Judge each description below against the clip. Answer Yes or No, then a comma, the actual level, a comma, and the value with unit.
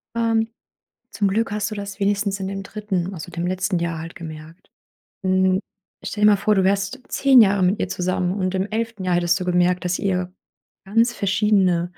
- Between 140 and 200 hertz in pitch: Yes, high, 190 Hz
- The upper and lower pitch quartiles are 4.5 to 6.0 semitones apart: No, narrow, 2.5 semitones